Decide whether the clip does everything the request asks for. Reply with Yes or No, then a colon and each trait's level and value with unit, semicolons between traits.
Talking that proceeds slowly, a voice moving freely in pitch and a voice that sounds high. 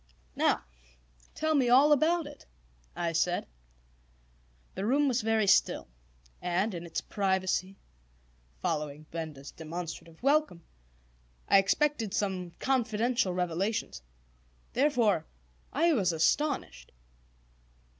Yes: slow, 100 wpm; wide, 7.6 semitones; high, 200 Hz